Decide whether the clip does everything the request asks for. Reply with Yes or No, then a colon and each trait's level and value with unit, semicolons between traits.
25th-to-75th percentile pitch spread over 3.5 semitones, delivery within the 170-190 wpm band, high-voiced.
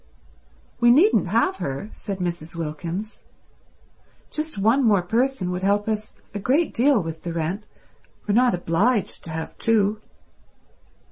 No: wide, 5.4 semitones; average, 140 wpm; high, 205 Hz